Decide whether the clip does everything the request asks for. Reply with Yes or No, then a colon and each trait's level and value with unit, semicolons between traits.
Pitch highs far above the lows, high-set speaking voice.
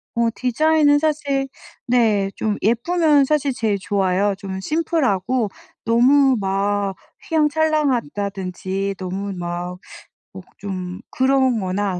Yes: wide, 6.3 semitones; high, 220 Hz